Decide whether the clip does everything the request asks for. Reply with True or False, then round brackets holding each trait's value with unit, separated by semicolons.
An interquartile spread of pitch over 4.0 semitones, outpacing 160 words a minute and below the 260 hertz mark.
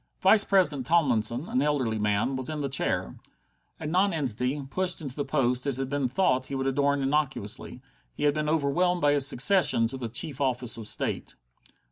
False (3.2 semitones; 190 wpm; 140 Hz)